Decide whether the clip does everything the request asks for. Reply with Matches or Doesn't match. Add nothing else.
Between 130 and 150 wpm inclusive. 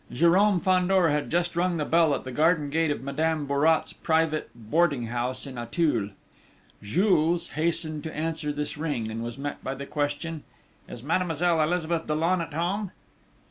Doesn't match